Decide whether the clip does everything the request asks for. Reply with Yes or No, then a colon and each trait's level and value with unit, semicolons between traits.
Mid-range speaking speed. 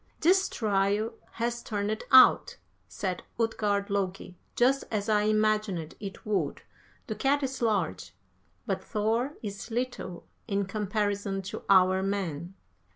No: slow, 125 wpm